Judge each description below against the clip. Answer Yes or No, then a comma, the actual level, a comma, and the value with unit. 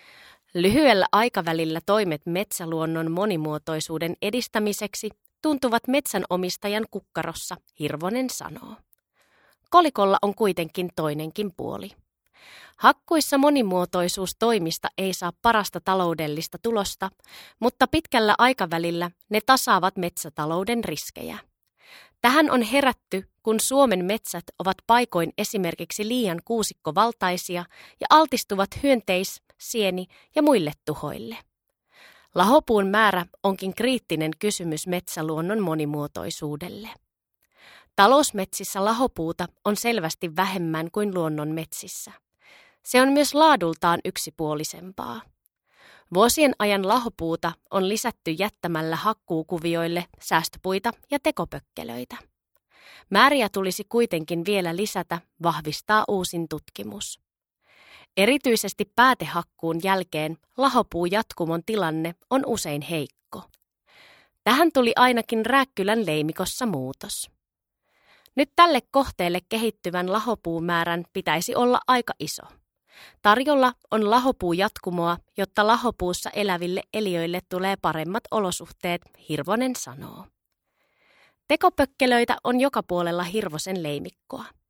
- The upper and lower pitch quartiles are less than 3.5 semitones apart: No, wide, 5.4 semitones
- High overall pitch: Yes, high, 195 Hz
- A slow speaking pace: Yes, slow, 90 wpm